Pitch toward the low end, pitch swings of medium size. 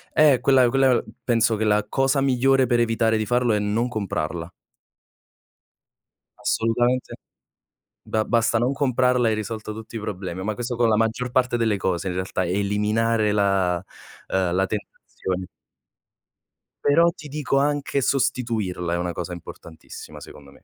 Yes: low, 115 Hz; average, 4.3 semitones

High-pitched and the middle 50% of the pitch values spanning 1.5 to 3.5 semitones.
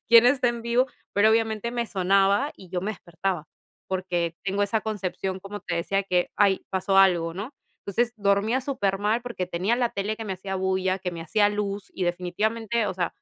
Yes: high, 200 Hz; average, 2.9 semitones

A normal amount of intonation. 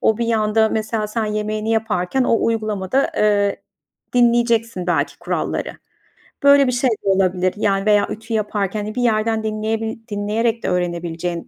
No: narrow, 2.1 semitones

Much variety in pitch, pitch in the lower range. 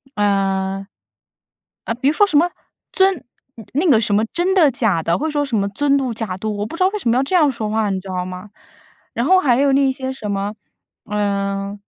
No: wide, 6.2 semitones; high, 225 Hz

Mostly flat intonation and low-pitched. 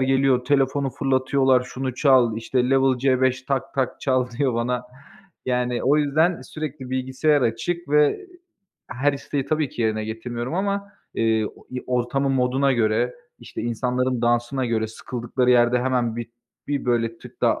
Yes: narrow, 2.3 semitones; low, 130 Hz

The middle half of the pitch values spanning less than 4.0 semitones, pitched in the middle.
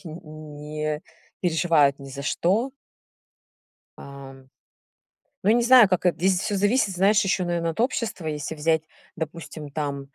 No: average, 4.3 semitones; medium, 165 Hz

